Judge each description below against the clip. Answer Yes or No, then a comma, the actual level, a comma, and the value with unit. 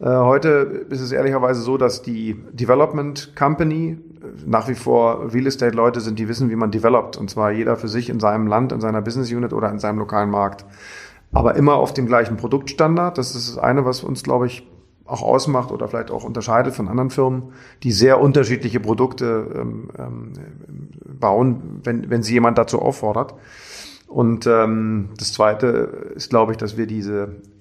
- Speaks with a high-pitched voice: No, low, 120 Hz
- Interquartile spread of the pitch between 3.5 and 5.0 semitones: No, average, 2.8 semitones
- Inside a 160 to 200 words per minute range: Yes, average, 170 wpm